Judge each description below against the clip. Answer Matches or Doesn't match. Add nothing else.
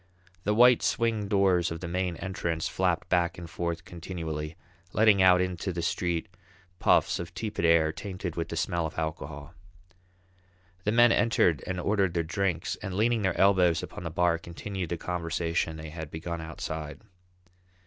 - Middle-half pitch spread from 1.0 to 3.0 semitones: Matches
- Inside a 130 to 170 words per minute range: Matches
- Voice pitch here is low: Matches